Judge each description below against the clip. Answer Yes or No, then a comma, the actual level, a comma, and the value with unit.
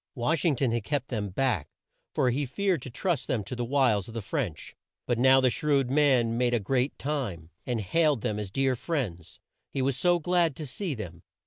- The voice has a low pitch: Yes, low, 130 Hz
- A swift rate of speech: Yes, fast, 215 wpm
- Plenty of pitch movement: No, average, 4.2 semitones